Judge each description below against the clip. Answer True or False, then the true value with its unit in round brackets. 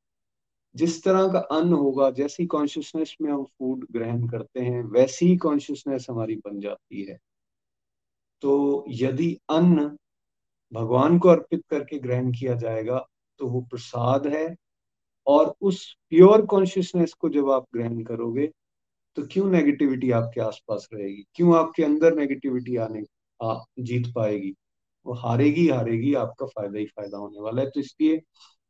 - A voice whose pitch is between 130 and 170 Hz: True (135 Hz)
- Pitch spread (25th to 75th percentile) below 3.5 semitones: False (5.4 semitones)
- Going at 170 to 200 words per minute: False (140 wpm)